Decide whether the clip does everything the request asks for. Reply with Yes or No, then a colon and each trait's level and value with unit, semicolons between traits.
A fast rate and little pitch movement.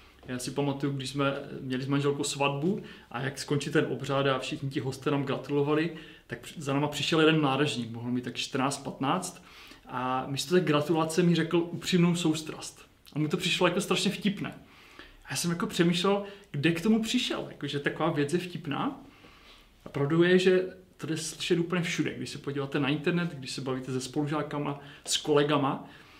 No: fast, 185 wpm; average, 3.8 semitones